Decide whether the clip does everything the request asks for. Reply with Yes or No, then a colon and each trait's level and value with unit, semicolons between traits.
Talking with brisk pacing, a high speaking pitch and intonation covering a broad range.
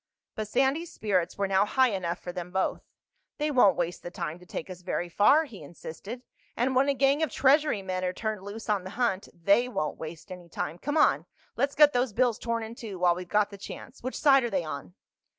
Yes: fast, 230 wpm; high, 205 Hz; wide, 6.0 semitones